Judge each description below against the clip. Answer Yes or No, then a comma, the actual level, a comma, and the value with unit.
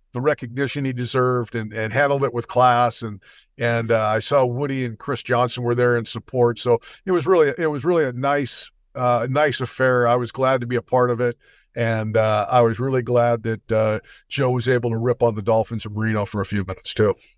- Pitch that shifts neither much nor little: No, narrow, 2.2 semitones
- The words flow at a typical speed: No, fast, 235 wpm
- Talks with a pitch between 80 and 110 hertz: No, low, 120 Hz